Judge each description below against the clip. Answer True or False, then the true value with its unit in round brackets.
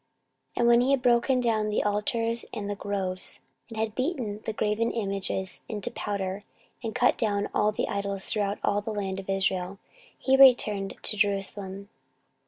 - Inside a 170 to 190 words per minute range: True (175 wpm)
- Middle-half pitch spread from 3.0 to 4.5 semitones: False (2.5 semitones)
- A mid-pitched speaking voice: False (210 Hz)